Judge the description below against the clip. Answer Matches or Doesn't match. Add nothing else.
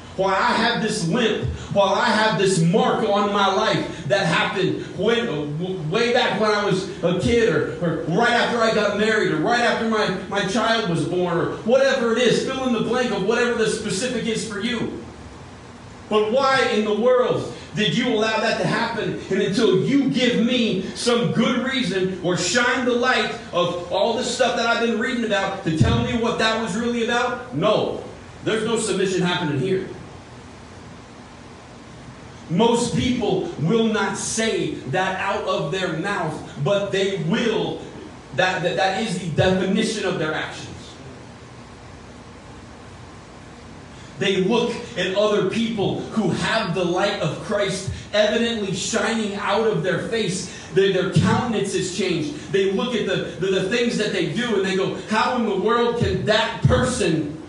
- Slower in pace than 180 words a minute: Matches